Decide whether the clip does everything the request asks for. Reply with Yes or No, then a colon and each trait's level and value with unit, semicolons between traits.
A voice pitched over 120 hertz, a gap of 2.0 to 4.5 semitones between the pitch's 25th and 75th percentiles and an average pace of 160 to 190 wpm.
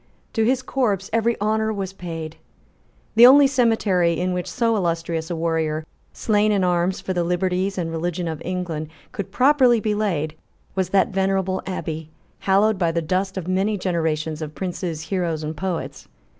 Yes: medium, 185 Hz; average, 3.9 semitones; average, 170 wpm